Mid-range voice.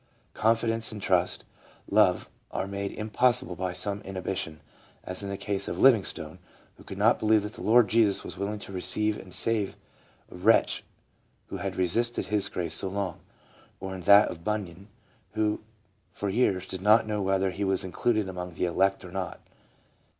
No: low, 100 Hz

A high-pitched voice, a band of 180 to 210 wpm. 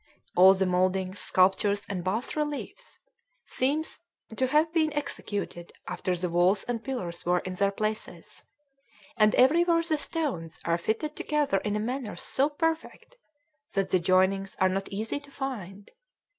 No: high, 210 Hz; average, 155 wpm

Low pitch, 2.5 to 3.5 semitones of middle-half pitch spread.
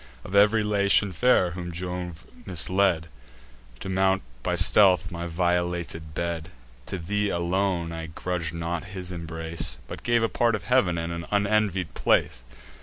Yes: very low, 90 Hz; average, 2.9 semitones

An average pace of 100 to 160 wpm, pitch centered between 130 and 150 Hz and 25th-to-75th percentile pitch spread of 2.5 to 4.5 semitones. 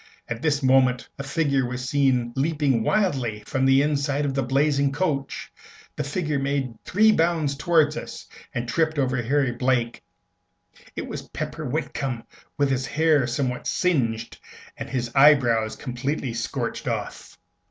Yes: average, 145 wpm; low, 135 Hz; average, 3.0 semitones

